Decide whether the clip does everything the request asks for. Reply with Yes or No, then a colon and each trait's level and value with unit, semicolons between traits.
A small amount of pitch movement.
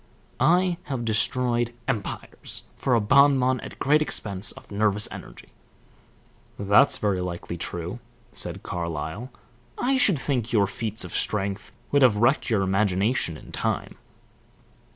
No: average, 5.0 semitones